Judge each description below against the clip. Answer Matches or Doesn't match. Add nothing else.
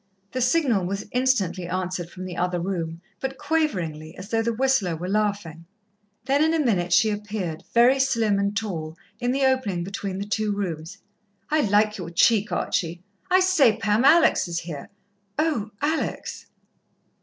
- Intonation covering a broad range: Matches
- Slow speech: Doesn't match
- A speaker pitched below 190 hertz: Doesn't match